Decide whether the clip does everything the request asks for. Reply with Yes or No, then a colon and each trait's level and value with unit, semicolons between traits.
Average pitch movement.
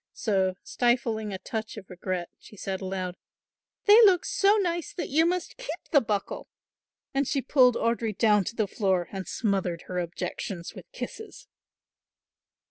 No: wide, 7.2 semitones